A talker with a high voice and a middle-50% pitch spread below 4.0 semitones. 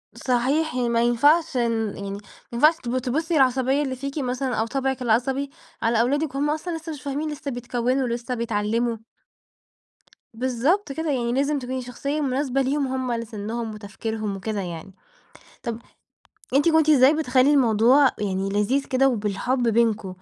Yes: very high, 255 Hz; average, 3.4 semitones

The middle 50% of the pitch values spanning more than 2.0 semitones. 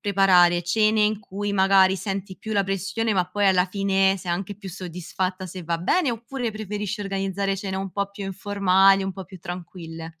No: narrow, 1.7 semitones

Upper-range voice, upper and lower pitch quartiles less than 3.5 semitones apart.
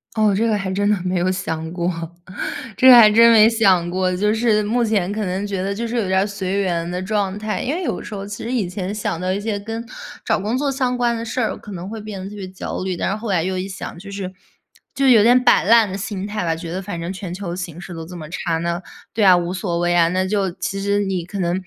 Yes: high, 195 Hz; average, 2.9 semitones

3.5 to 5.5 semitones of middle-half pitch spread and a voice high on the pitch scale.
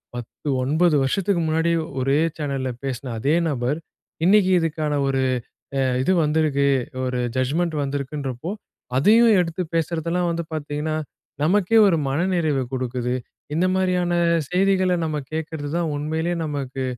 No: average, 4.1 semitones; medium, 155 Hz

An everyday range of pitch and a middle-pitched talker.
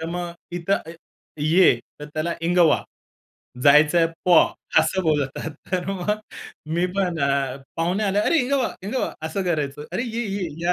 Yes: average, 3.8 semitones; medium, 175 Hz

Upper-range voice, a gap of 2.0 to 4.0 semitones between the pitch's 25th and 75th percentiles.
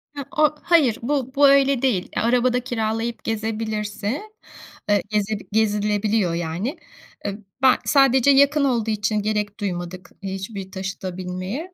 No: high, 220 Hz; average, 4.4 semitones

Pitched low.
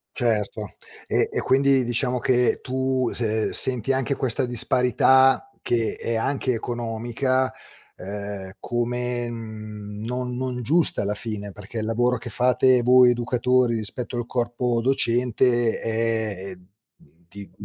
Yes: low, 120 Hz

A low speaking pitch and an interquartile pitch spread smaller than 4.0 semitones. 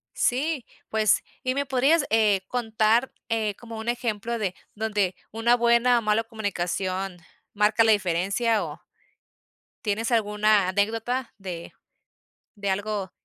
No: high, 220 Hz; average, 2.8 semitones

